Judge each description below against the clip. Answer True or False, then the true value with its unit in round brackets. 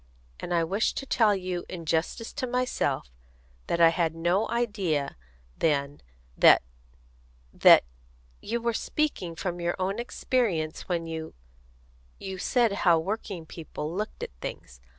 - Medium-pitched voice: True (180 Hz)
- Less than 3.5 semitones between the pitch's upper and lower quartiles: False (5.2 semitones)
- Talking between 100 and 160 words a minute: True (140 wpm)